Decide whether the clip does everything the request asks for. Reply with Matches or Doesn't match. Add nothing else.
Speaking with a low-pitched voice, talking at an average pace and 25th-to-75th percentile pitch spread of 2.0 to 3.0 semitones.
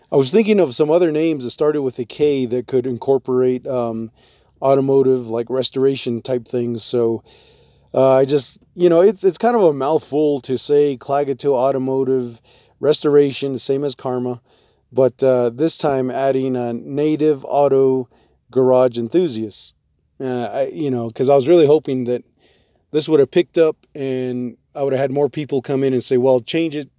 Matches